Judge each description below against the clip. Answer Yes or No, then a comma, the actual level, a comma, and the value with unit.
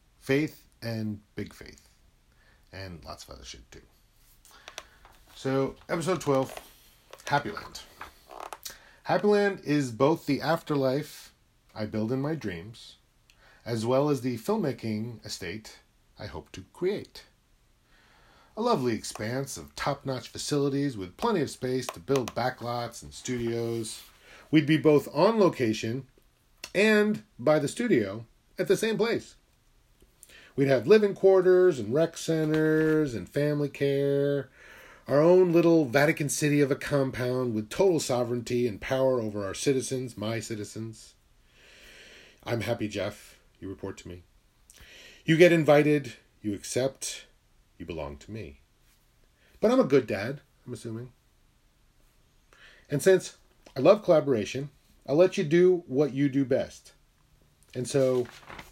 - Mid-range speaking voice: No, low, 130 Hz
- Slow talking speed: Yes, slow, 130 wpm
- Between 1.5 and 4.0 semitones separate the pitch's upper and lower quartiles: No, average, 5.1 semitones